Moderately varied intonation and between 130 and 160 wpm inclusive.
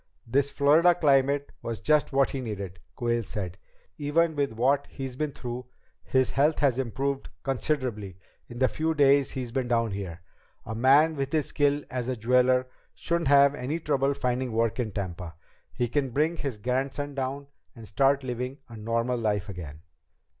No: average, 3.5 semitones; average, 170 wpm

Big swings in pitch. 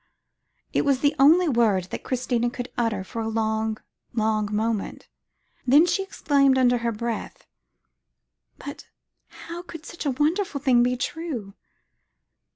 No: average, 4.7 semitones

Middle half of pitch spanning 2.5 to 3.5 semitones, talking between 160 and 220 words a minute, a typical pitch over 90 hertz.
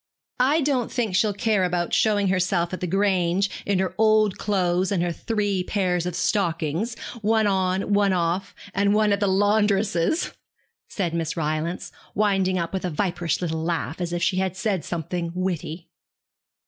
Yes: average, 2.9 semitones; average, 170 wpm; high, 190 Hz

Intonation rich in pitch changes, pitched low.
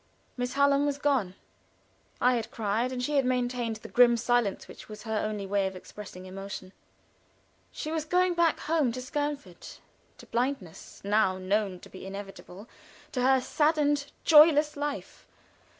No: wide, 6.1 semitones; high, 245 Hz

